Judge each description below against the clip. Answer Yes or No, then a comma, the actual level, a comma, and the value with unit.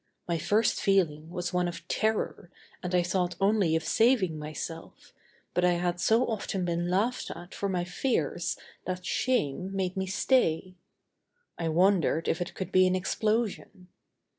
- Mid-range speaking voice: Yes, medium, 180 Hz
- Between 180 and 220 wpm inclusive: No, average, 160 wpm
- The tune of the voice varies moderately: No, narrow, 2.3 semitones